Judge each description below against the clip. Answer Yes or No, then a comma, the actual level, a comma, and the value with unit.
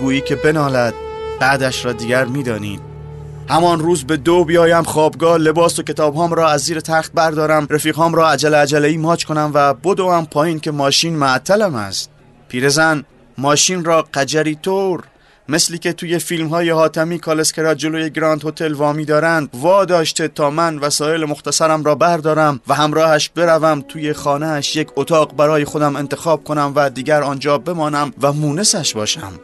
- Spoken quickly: Yes, fast, 165 wpm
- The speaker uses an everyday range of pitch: No, narrow, 2.1 semitones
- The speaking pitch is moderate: Yes, medium, 155 Hz